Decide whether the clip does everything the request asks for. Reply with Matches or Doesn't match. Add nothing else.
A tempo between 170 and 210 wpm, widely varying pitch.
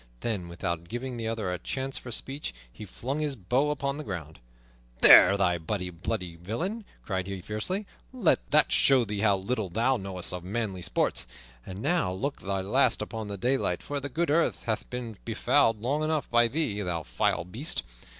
Matches